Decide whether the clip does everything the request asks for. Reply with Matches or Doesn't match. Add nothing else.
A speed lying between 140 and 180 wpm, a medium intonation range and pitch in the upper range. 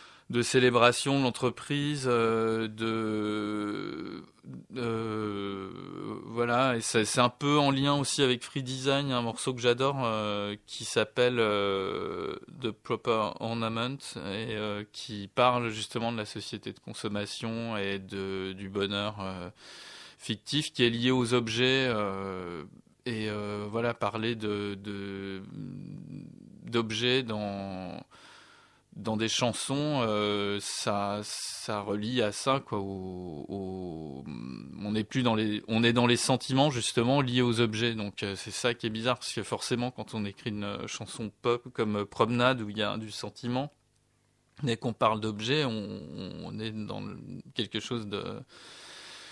Doesn't match